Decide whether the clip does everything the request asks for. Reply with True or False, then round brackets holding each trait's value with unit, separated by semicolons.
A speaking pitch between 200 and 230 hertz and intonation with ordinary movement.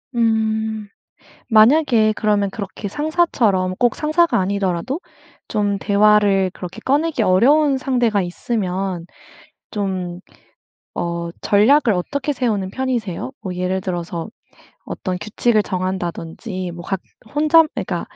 True (210 Hz; 4.8 semitones)